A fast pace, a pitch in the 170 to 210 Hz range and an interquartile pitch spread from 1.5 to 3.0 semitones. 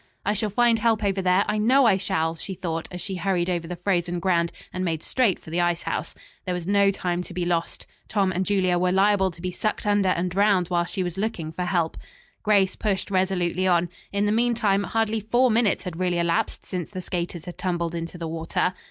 Yes: fast, 225 wpm; medium, 185 Hz; average, 2.7 semitones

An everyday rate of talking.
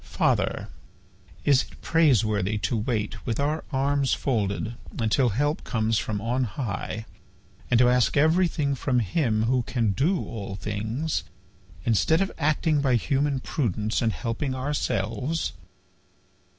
No: slow, 130 wpm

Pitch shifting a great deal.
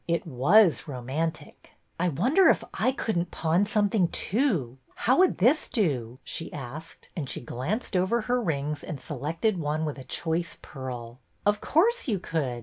Yes: wide, 7.3 semitones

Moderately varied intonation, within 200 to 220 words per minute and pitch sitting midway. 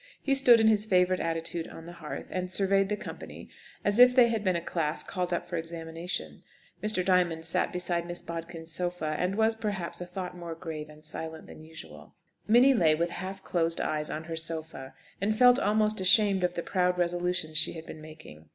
Yes: average, 3.3 semitones; fast, 205 wpm; medium, 175 Hz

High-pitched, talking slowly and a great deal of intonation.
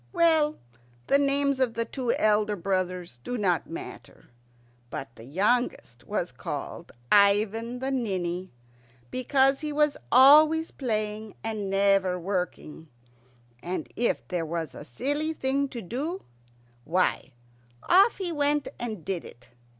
Yes: high, 220 Hz; slow, 130 wpm; wide, 7.1 semitones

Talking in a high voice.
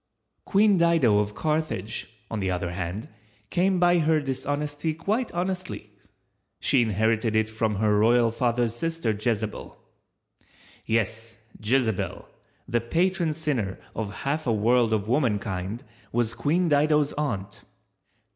No: low, 120 Hz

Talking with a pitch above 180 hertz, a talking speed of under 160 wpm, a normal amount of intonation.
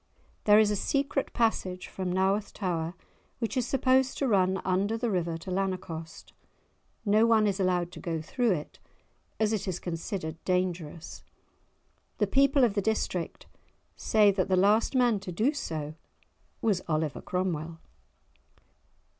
Yes: high, 190 Hz; average, 145 wpm; average, 3.9 semitones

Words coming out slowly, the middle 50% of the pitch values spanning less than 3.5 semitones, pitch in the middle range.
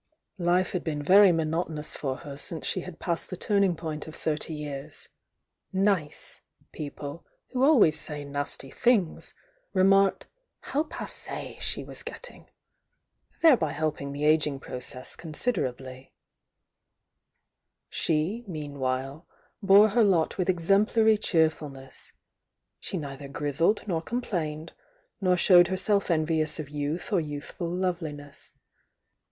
No: slow, 115 wpm; average, 4.3 semitones; medium, 160 Hz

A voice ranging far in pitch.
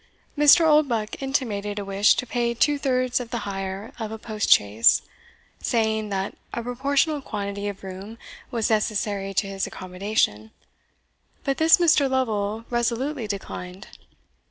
No: average, 4.2 semitones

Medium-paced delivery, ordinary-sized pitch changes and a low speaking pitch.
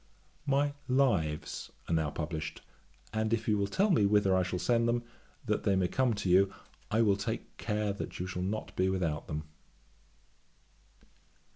Yes: average, 170 wpm; average, 4.0 semitones; low, 100 Hz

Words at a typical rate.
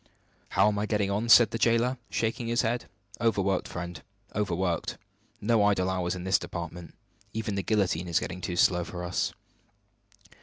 Yes: average, 165 wpm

